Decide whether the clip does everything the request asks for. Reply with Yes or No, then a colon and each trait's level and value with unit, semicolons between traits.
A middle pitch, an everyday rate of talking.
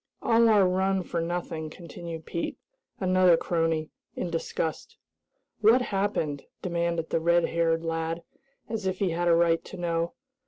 Yes: medium, 170 Hz; average, 150 wpm